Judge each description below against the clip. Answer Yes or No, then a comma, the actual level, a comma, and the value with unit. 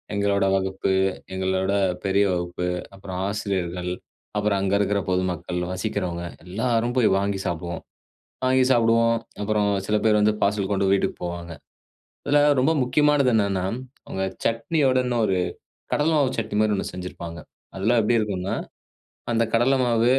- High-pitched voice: No, low, 100 Hz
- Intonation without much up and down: No, average, 3.7 semitones